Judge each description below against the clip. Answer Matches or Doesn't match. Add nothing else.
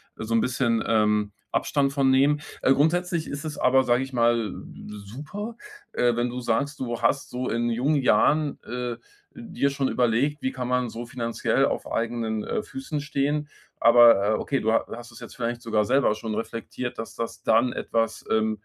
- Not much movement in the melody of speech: Doesn't match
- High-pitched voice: Doesn't match